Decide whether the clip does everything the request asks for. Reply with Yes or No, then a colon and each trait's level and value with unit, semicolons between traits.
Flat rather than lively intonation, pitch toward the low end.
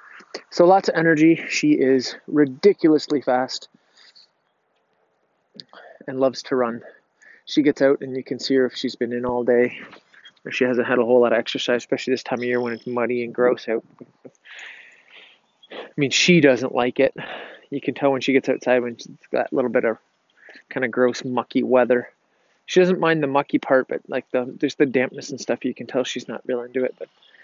Yes: narrow, 2.3 semitones; low, 130 Hz